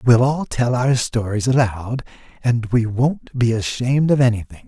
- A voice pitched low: Yes, low, 120 Hz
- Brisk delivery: No, average, 165 wpm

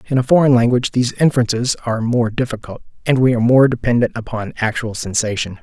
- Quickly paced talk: No, average, 180 wpm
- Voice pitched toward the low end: Yes, low, 120 Hz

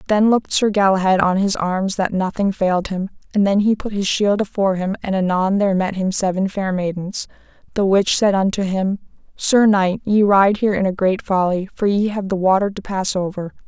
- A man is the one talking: No, female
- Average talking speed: No, fast, 215 wpm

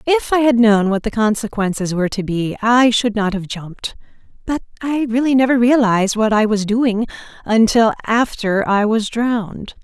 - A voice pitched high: Yes, high, 225 Hz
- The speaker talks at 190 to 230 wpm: No, average, 175 wpm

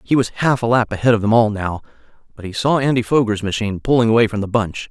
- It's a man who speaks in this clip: Yes, male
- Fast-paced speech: Yes, fast, 255 wpm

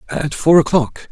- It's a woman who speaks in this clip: No, male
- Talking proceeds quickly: No, average, 160 wpm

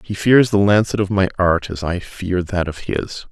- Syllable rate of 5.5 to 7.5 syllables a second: No, 4.5 syllables/s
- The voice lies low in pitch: Yes, very low, 95 Hz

